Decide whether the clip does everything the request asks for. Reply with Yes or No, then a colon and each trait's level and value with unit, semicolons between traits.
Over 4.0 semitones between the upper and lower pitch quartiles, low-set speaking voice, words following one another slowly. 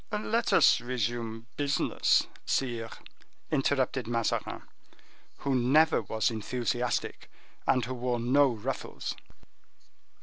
No: average, 2.7 semitones; low, 125 Hz; slow, 95 wpm